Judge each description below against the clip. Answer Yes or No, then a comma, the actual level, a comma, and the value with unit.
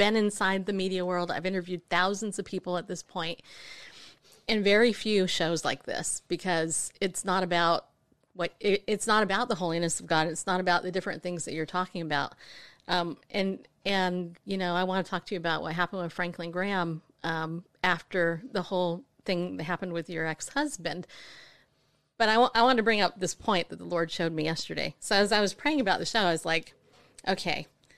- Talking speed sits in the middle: No, fast, 210 wpm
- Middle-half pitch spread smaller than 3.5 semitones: Yes, narrow, 2.6 semitones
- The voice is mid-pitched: Yes, medium, 180 Hz